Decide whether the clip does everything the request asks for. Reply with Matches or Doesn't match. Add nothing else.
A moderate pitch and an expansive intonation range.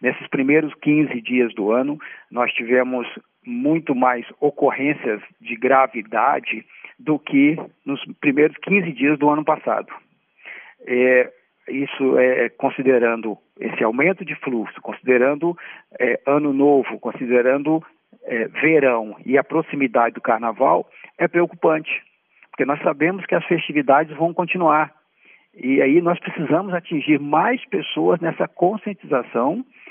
Doesn't match